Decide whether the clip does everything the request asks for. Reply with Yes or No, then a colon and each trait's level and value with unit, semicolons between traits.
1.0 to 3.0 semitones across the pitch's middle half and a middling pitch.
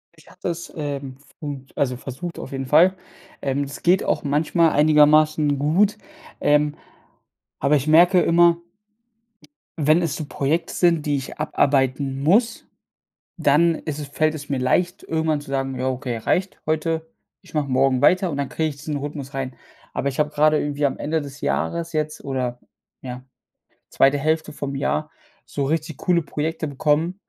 Yes: average, 2.7 semitones; medium, 150 Hz